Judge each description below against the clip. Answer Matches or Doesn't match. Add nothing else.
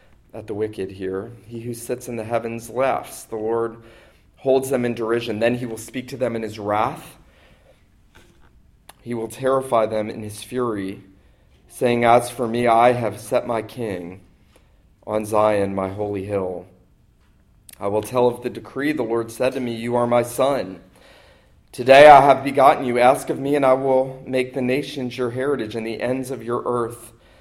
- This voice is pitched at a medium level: Doesn't match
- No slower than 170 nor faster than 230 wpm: Matches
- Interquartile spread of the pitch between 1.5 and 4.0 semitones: Matches